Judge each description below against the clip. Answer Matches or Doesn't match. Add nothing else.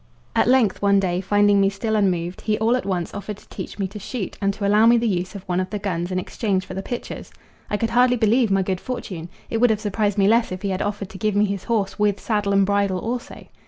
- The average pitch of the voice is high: Matches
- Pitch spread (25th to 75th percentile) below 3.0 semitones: Matches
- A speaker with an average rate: Doesn't match